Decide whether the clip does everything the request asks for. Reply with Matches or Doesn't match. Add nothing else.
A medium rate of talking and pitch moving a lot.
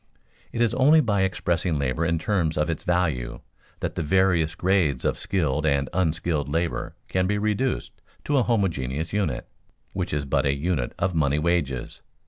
Doesn't match